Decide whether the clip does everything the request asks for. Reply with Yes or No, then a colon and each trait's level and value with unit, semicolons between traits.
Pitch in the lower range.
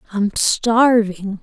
No: high, 215 Hz